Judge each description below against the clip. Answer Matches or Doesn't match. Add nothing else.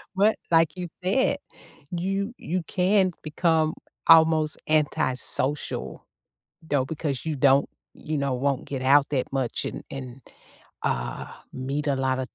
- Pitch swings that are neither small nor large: Matches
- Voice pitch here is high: Doesn't match